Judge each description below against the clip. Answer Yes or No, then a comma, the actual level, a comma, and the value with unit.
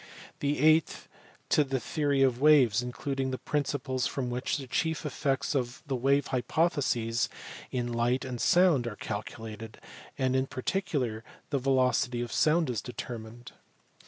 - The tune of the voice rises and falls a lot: No, average, 2.9 semitones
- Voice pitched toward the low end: Yes, low, 130 Hz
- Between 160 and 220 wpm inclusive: No, average, 145 wpm